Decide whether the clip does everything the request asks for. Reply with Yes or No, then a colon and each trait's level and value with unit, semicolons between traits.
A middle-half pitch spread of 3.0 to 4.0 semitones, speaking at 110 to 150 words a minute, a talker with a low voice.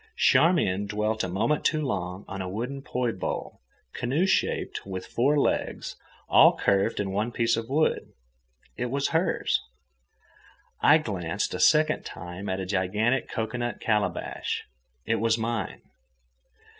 No: wide, 5.4 semitones; average, 140 wpm; low, 115 Hz